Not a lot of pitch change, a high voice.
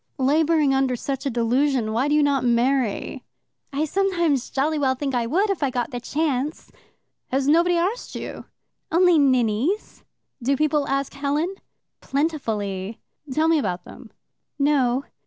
No: average, 3.6 semitones; very high, 275 Hz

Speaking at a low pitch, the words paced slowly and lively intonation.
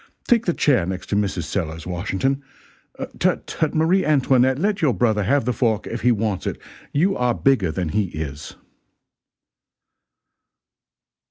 No: low, 120 Hz; average, 150 wpm; wide, 7.2 semitones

